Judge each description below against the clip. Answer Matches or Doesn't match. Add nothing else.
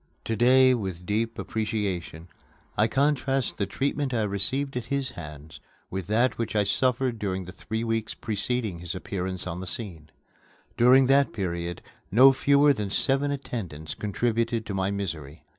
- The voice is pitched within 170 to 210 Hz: Doesn't match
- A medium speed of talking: Matches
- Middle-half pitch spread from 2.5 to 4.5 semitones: Doesn't match